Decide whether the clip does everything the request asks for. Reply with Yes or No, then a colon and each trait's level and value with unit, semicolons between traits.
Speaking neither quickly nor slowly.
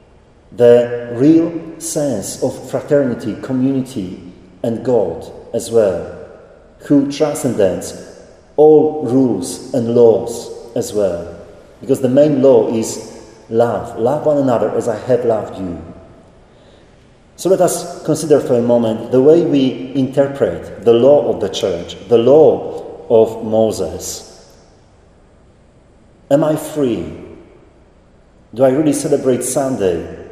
No: slow, 120 wpm